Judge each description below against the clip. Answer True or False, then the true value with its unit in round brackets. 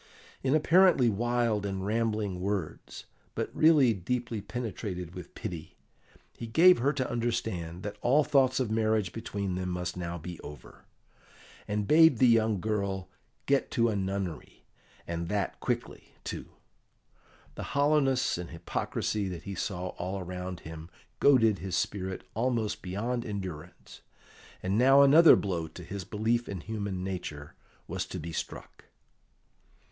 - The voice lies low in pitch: True (105 Hz)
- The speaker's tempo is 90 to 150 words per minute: True (140 wpm)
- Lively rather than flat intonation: False (4.8 semitones)